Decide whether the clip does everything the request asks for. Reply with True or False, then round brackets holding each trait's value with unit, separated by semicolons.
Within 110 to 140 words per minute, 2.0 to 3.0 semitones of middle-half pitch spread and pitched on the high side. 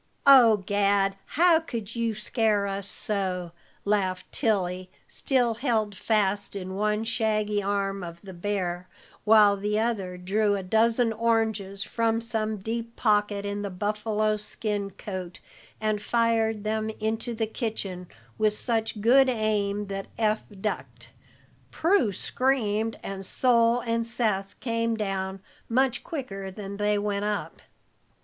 True (135 wpm; 2.5 semitones; 210 Hz)